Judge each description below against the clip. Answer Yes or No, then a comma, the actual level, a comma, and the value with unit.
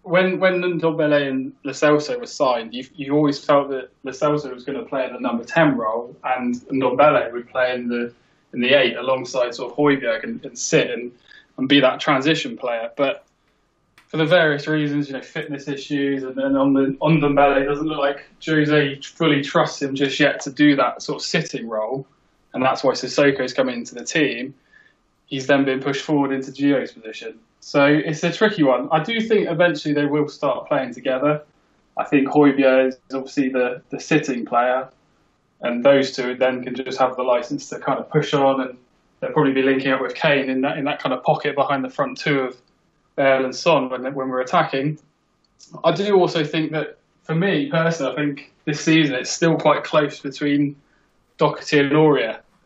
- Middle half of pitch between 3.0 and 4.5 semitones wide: No, narrow, 2.6 semitones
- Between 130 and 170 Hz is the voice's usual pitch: Yes, medium, 140 Hz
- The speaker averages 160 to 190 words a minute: No, average, 200 wpm